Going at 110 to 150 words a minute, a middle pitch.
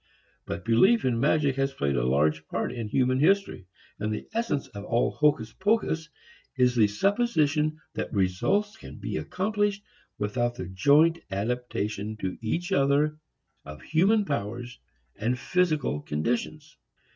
No: average, 140 wpm; low, 130 Hz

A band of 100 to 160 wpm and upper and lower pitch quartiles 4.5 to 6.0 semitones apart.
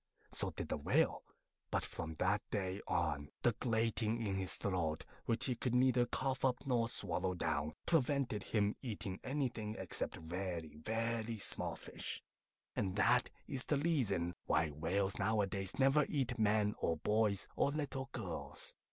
Yes: average, 150 wpm; average, 4.9 semitones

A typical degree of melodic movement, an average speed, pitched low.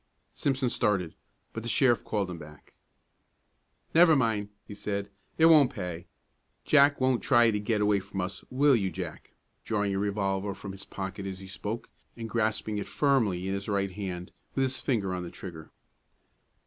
Yes: average, 3.7 semitones; average, 175 wpm; low, 105 Hz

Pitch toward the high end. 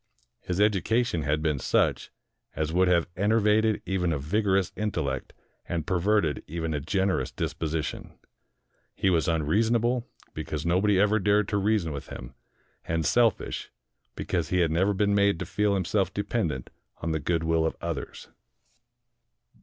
No: very low, 90 Hz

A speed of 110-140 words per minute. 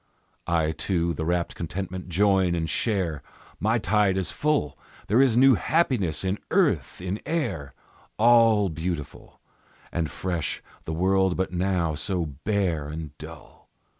Yes: slow, 135 wpm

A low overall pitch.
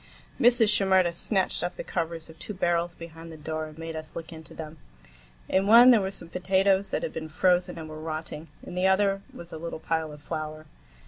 No: medium, 170 Hz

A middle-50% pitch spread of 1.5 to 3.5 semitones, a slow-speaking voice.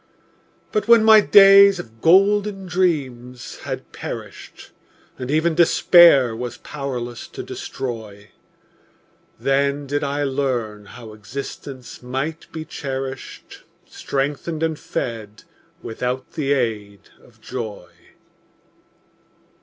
No: average, 5.1 semitones; slow, 100 wpm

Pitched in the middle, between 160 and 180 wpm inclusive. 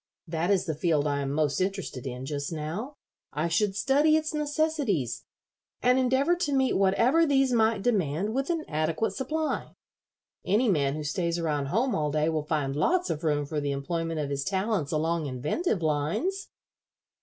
Yes: medium, 170 Hz; average, 175 wpm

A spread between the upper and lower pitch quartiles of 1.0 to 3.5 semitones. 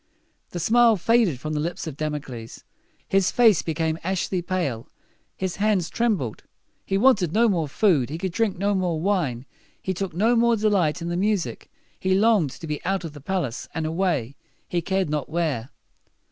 No: average, 4.5 semitones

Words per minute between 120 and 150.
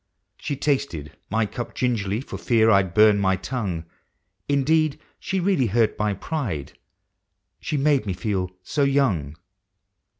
Yes: average, 140 wpm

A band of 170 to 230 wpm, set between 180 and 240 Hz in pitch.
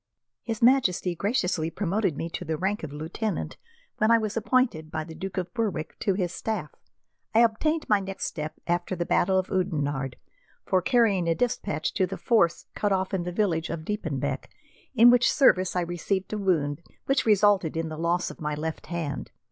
Yes: average, 190 wpm; medium, 185 Hz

